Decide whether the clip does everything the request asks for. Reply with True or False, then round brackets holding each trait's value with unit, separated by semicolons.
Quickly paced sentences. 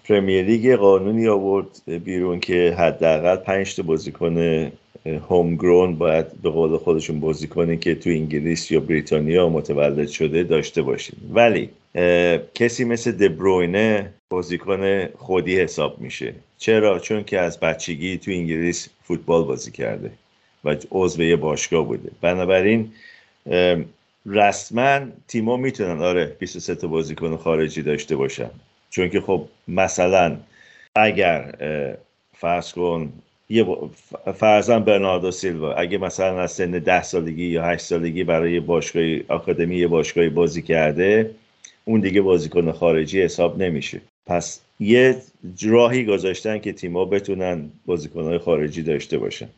False (125 wpm)